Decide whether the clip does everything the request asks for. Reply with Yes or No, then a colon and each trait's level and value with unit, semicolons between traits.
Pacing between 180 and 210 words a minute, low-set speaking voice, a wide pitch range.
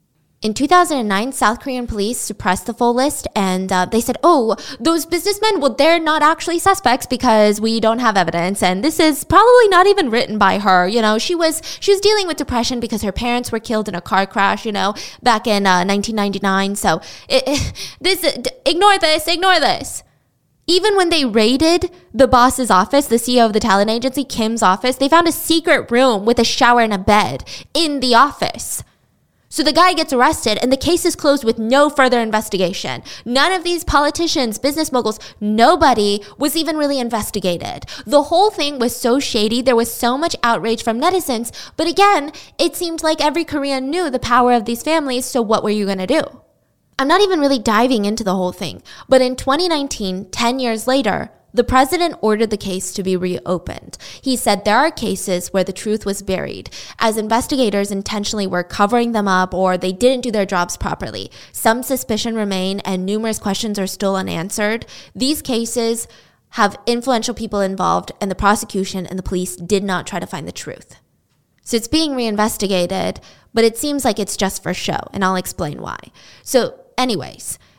No: average, 190 wpm; high, 235 Hz; wide, 6.1 semitones